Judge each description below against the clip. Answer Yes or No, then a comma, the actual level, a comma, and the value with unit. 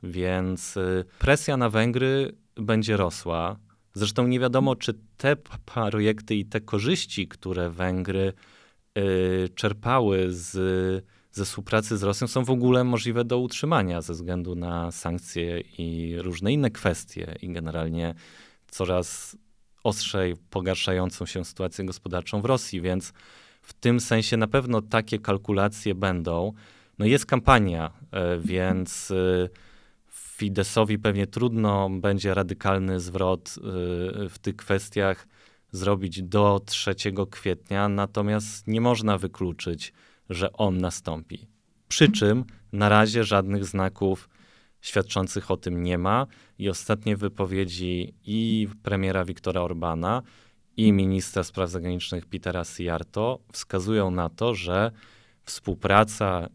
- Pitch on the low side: Yes, low, 100 Hz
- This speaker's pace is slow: No, average, 120 wpm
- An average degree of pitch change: Yes, average, 3.0 semitones